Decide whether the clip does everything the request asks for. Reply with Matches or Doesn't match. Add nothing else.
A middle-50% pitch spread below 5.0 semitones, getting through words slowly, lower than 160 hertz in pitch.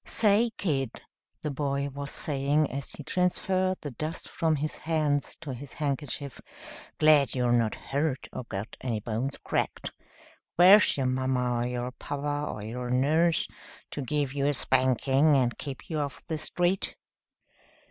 Doesn't match